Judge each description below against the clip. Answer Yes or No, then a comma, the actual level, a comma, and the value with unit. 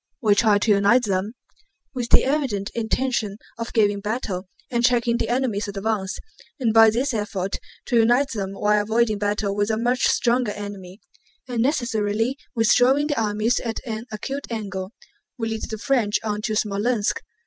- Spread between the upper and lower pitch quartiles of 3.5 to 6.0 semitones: No, average, 2.7 semitones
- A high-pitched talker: Yes, high, 220 Hz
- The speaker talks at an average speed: Yes, average, 160 wpm